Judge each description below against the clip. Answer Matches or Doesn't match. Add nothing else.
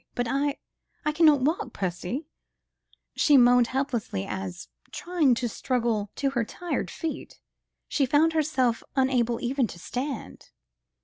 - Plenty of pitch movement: Doesn't match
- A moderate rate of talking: Doesn't match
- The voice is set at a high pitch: Matches